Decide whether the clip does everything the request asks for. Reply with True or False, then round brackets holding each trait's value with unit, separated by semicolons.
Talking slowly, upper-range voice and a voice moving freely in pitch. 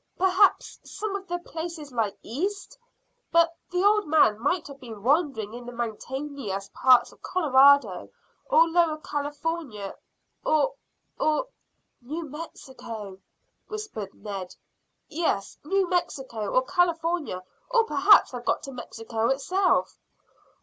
True (125 wpm; 290 Hz; 6.8 semitones)